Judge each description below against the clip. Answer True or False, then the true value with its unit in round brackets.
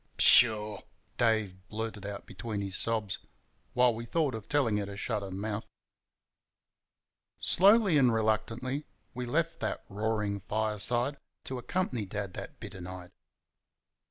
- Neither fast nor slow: False (130 wpm)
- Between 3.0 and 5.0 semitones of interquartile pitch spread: True (3.4 semitones)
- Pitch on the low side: True (110 Hz)